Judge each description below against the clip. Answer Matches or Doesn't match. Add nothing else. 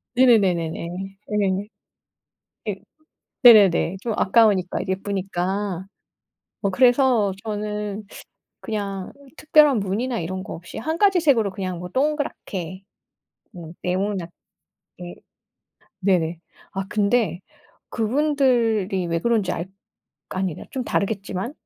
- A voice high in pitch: Matches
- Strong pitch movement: Doesn't match